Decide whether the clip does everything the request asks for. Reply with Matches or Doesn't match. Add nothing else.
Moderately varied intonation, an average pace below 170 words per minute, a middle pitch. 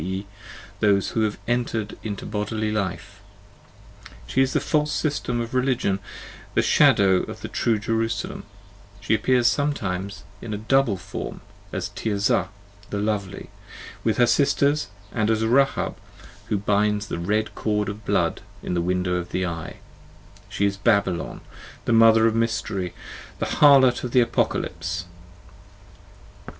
Doesn't match